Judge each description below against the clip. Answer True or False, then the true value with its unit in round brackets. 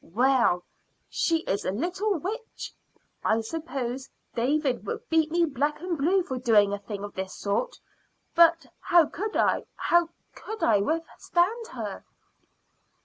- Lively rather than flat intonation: True (6.9 semitones)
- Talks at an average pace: True (145 wpm)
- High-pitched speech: True (305 Hz)